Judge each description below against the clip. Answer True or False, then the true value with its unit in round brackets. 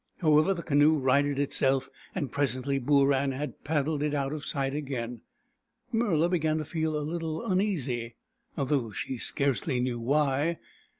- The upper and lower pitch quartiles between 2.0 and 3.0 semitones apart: True (2.7 semitones)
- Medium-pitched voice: True (145 Hz)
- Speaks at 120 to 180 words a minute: True (155 wpm)